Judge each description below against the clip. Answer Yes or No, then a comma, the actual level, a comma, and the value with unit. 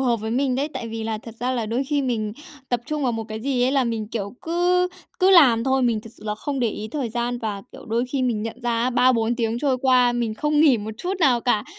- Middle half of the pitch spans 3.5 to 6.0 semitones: No, average, 3.0 semitones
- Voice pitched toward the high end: Yes, high, 240 Hz